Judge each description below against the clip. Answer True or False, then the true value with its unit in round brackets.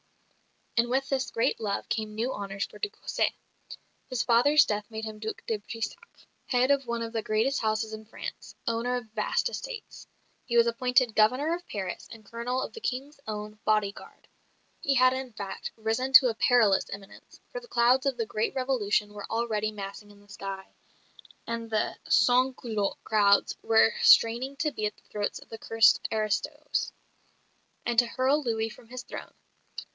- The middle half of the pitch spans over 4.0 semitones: False (3.0 semitones)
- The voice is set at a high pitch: True (230 Hz)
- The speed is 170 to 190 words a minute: True (180 wpm)